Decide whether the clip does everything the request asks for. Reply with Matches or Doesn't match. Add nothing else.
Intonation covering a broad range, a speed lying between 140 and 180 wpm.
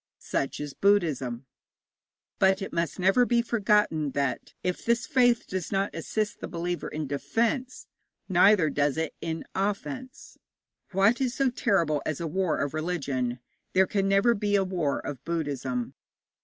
Matches